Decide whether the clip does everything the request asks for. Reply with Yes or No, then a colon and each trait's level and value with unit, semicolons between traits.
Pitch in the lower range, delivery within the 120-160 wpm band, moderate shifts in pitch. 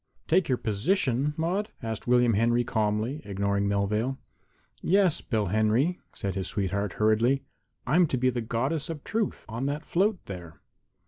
No: low, 120 Hz; average, 150 wpm; wide, 6.1 semitones